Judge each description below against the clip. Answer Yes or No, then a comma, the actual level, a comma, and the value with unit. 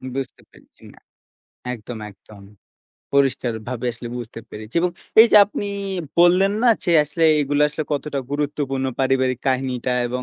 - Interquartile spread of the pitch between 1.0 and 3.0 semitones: No, average, 3.4 semitones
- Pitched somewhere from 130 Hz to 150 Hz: Yes, low, 135 Hz